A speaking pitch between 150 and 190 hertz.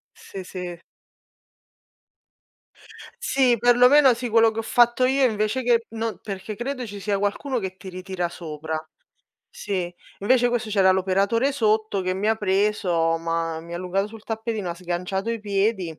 No: high, 205 Hz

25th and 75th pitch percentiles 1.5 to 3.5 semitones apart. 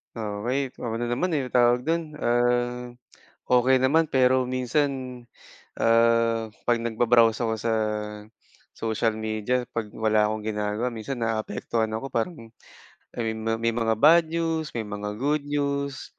Yes: average, 2.7 semitones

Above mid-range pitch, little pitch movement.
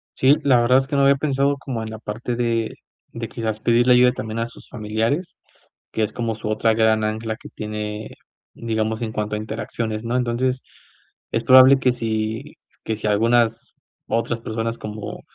No: low, 115 Hz; narrow, 2.2 semitones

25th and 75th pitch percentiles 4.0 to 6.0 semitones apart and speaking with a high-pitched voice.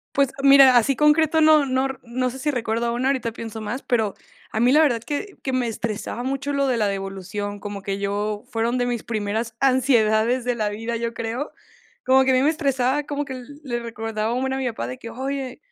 No: average, 3.4 semitones; high, 245 Hz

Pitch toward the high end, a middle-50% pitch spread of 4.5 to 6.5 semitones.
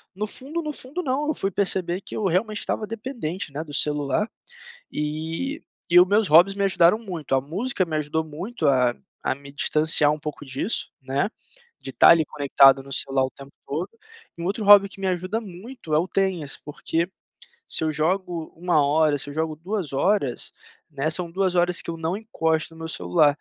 No: medium, 170 Hz; average, 4.8 semitones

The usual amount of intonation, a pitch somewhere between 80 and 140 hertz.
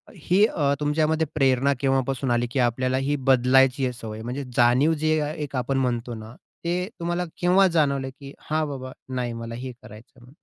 Yes: average, 3.6 semitones; low, 135 Hz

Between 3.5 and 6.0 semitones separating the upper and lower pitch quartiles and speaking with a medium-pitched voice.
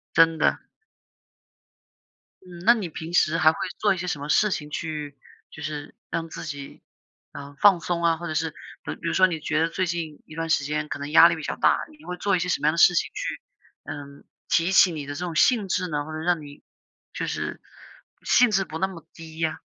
No: average, 2.8 semitones; medium, 165 Hz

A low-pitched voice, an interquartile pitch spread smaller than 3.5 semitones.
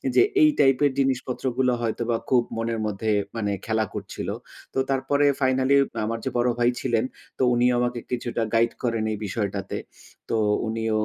Yes: low, 120 Hz; narrow, 2.6 semitones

